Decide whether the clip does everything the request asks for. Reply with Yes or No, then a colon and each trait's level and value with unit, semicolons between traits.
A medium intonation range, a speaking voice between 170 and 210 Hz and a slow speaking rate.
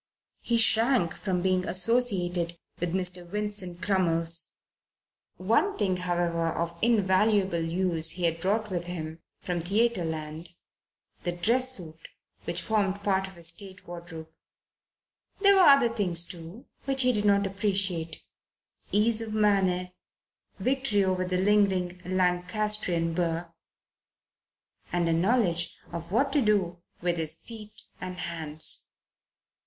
Yes: average, 3.6 semitones; medium, 185 Hz; slow, 125 wpm